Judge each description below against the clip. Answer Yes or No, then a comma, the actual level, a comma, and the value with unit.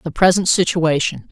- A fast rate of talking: No, slow, 135 wpm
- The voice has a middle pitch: Yes, medium, 170 Hz